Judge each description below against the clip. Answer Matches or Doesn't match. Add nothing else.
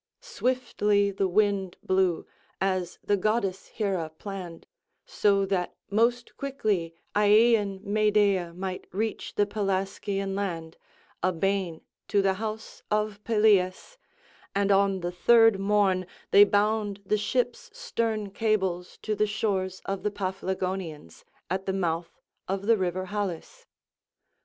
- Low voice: Doesn't match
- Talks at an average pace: Doesn't match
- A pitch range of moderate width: Doesn't match